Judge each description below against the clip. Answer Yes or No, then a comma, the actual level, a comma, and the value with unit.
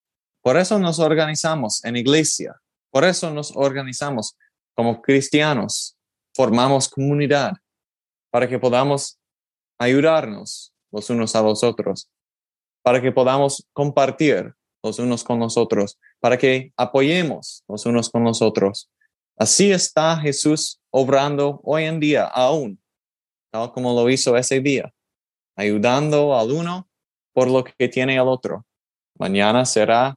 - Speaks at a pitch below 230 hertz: Yes, low, 135 Hz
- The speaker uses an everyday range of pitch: Yes, average, 3.6 semitones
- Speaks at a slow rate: Yes, slow, 130 wpm